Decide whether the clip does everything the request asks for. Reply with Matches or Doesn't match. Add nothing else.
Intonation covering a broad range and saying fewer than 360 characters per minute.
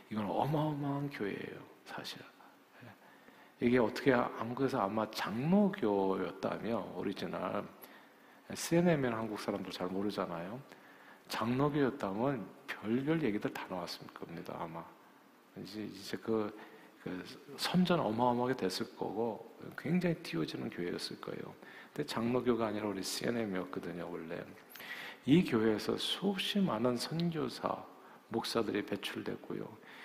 Matches